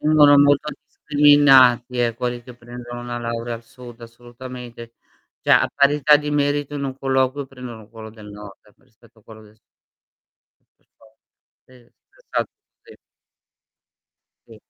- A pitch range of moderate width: Yes, average, 3.4 semitones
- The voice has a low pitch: Yes, low, 125 Hz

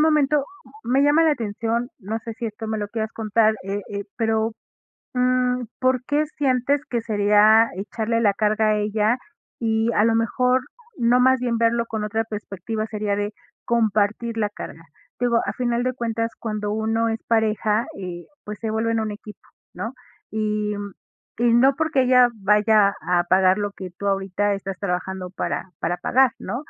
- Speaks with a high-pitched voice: Yes, high, 220 Hz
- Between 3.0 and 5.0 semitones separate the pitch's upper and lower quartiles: No, narrow, 2.5 semitones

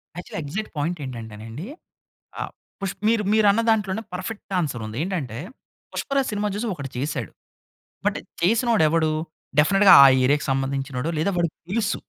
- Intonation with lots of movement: Yes, wide, 7.3 semitones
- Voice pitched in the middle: Yes, medium, 170 Hz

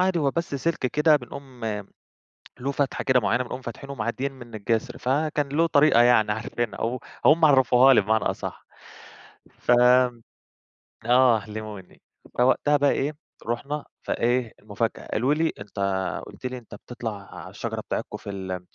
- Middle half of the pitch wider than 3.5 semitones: Yes, average, 4.0 semitones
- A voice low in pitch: Yes, low, 125 Hz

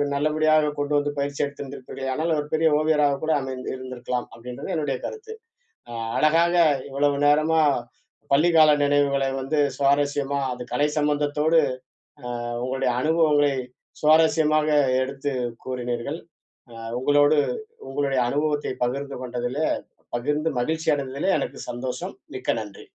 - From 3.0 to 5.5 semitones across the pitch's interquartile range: No, narrow, 2.6 semitones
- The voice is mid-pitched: Yes, medium, 145 Hz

